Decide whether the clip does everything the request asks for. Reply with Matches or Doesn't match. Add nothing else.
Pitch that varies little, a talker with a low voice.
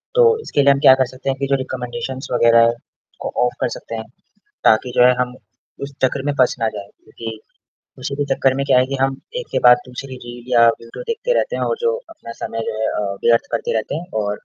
Doesn't match